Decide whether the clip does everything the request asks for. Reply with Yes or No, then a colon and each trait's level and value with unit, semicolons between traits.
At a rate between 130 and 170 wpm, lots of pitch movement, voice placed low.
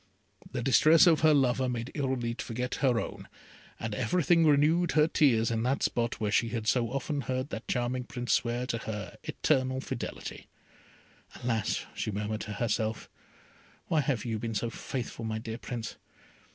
No: average, 165 wpm; average, 3.3 semitones; low, 120 Hz